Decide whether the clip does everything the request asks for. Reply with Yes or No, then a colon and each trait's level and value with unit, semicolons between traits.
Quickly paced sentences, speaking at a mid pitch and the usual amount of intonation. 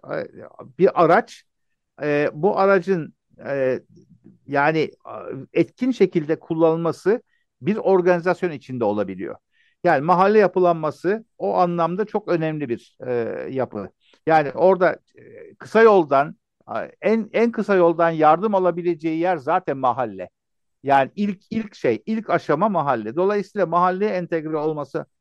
No: average, 105 wpm; medium, 175 Hz; average, 4.6 semitones